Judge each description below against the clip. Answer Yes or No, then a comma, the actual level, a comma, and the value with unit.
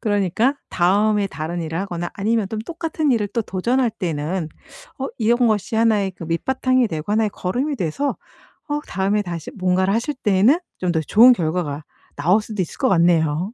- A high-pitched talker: Yes, high, 200 Hz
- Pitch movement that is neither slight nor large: Yes, average, 4.9 semitones